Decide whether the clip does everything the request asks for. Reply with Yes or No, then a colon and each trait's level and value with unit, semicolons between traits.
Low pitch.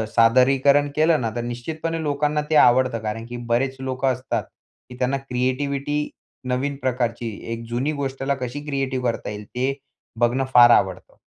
Yes: low, 130 Hz